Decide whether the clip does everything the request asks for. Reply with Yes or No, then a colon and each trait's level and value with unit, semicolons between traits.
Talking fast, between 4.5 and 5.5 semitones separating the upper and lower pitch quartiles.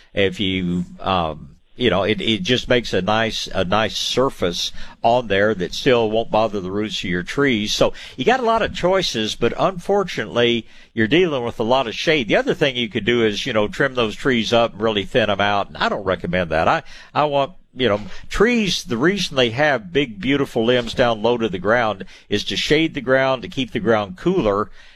Yes: fast, 220 wpm; average, 5.1 semitones